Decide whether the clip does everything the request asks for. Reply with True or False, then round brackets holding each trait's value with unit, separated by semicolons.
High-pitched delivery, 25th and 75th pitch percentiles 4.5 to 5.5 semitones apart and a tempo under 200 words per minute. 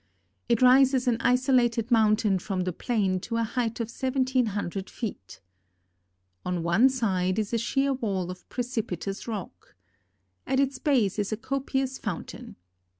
True (230 Hz; 4.8 semitones; 150 wpm)